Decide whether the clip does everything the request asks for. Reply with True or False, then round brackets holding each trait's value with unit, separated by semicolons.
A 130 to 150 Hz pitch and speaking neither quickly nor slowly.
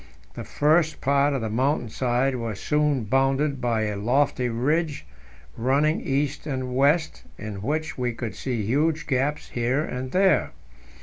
True (135 Hz; 150 wpm)